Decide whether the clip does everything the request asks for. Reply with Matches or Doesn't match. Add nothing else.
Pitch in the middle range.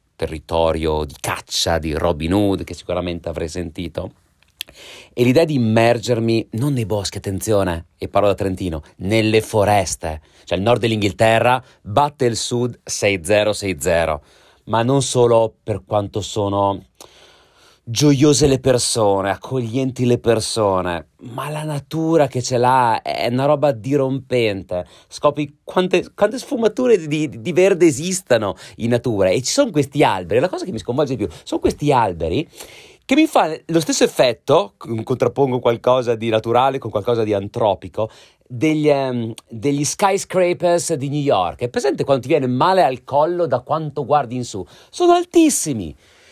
Doesn't match